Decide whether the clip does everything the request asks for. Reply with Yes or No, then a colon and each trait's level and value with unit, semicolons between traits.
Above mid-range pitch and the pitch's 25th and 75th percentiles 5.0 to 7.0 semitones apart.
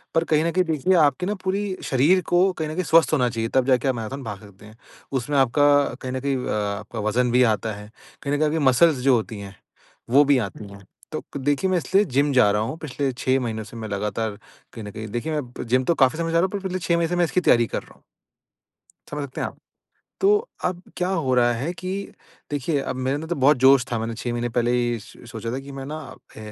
No: low, 130 Hz; wide, 5.4 semitones